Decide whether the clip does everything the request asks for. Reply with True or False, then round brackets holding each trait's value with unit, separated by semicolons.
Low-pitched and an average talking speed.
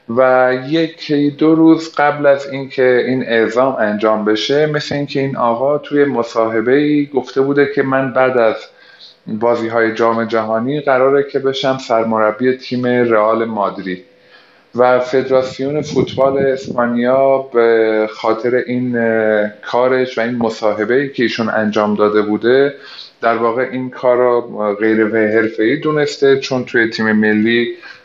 True (125 Hz; 140 wpm)